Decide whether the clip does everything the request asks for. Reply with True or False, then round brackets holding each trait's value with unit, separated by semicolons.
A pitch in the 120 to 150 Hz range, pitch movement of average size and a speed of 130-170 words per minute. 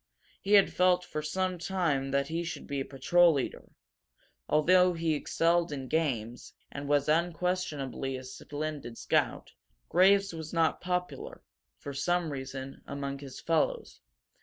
False (160 Hz; 4.4 semitones; 140 wpm)